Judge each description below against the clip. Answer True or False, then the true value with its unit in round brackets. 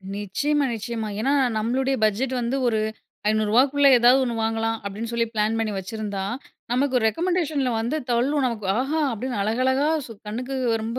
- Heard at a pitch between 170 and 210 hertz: False (235 Hz)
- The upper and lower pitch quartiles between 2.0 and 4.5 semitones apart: True (3.5 semitones)